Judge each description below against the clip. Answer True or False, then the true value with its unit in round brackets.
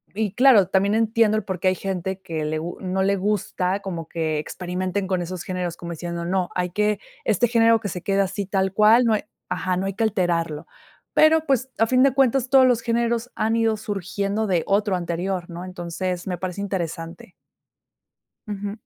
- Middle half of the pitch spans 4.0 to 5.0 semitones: False (3.4 semitones)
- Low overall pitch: False (195 Hz)